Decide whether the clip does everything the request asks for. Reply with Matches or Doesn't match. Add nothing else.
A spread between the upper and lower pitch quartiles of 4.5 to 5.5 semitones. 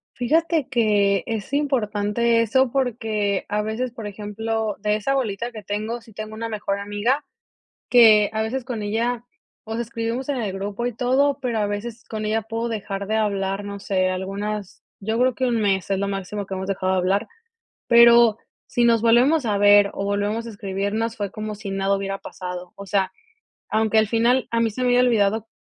Doesn't match